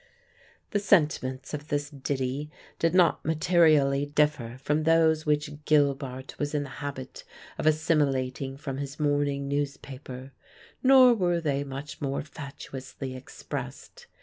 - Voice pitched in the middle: Yes, medium, 145 Hz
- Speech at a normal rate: No, slow, 125 wpm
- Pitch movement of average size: No, narrow, 2.3 semitones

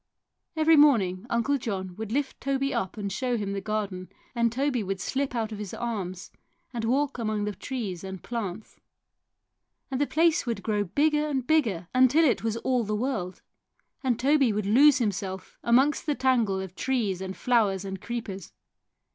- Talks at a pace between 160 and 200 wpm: Yes, average, 175 wpm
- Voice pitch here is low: No, high, 230 Hz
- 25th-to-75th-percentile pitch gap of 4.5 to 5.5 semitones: Yes, average, 5.1 semitones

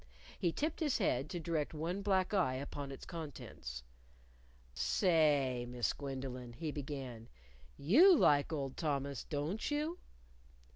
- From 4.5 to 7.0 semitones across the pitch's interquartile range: Yes, average, 5.1 semitones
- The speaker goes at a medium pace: No, slow, 130 wpm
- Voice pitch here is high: No, medium, 150 Hz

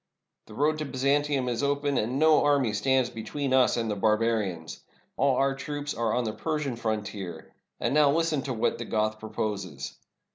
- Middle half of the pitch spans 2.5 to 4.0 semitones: No, average, 4.8 semitones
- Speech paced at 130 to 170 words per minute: No, average, 180 wpm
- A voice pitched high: No, low, 125 Hz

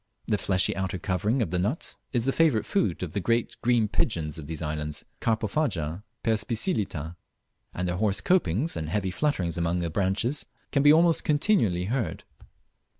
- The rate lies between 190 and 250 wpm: No, average, 165 wpm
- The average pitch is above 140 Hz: No, low, 100 Hz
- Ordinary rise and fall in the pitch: No, wide, 6.0 semitones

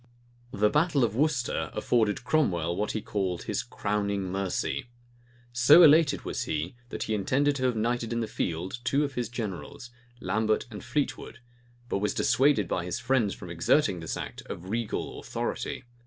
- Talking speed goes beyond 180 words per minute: No, average, 170 wpm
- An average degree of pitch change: Yes, average, 5.0 semitones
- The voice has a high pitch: No, low, 110 Hz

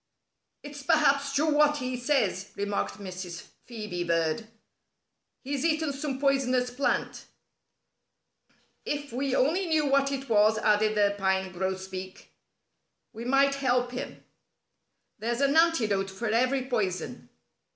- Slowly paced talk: Yes, slow, 120 wpm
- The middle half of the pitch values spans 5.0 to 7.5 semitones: Yes, wide, 5.6 semitones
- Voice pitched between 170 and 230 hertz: No, very high, 250 Hz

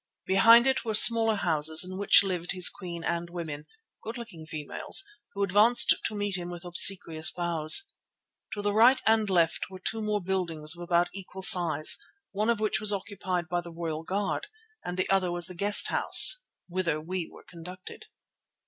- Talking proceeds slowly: No, average, 180 wpm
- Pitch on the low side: No, medium, 185 Hz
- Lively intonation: No, average, 3.2 semitones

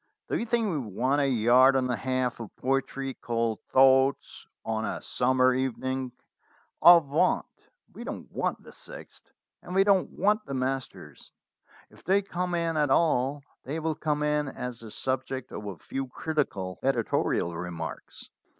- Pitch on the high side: No, low, 135 Hz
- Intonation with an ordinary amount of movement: Yes, average, 3.6 semitones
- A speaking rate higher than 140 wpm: Yes, average, 160 wpm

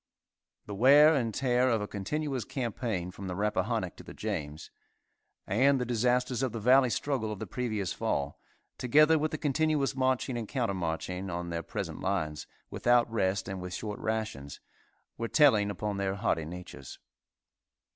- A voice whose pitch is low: Yes, low, 110 Hz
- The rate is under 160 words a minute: No, average, 165 wpm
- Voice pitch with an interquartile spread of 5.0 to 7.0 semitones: Yes, average, 5.3 semitones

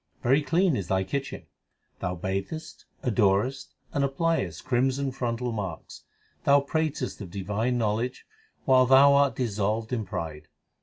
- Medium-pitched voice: No, low, 125 Hz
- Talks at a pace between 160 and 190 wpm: No, slow, 135 wpm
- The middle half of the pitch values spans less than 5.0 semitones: No, wide, 5.5 semitones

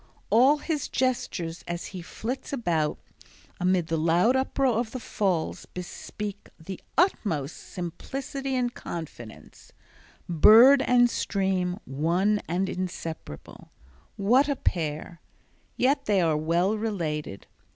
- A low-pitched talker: No, high, 190 Hz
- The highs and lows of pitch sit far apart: Yes, wide, 6.6 semitones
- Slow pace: Yes, slow, 110 wpm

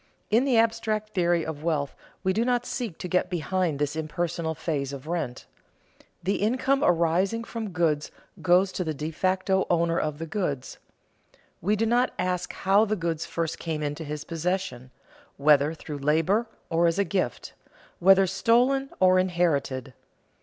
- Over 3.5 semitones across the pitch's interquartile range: Yes, average, 4.2 semitones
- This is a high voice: No, medium, 175 Hz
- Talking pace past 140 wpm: Yes, average, 160 wpm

